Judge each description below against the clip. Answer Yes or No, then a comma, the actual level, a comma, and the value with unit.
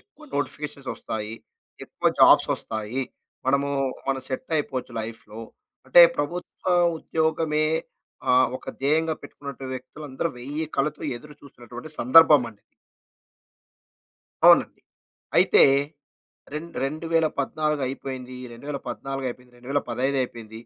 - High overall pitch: No, low, 135 Hz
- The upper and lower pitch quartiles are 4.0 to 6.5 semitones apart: No, average, 3.4 semitones